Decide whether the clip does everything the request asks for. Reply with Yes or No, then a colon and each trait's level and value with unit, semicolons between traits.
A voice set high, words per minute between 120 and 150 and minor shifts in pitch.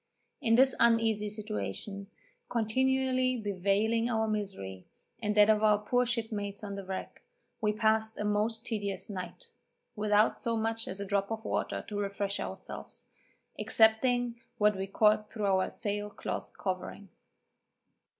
Yes: high, 210 Hz; average, 140 wpm; narrow, 2.1 semitones